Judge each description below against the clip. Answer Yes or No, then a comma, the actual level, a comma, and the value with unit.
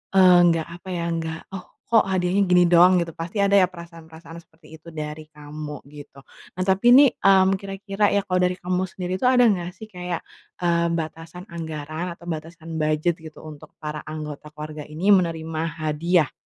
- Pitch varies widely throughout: No, average, 2.8 semitones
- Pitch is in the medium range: Yes, medium, 170 Hz